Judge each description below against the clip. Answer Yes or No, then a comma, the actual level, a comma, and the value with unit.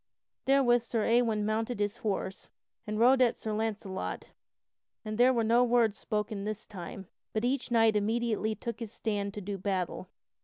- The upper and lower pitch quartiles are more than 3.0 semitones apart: No, narrow, 2.4 semitones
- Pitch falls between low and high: No, high, 220 Hz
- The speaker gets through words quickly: No, average, 165 wpm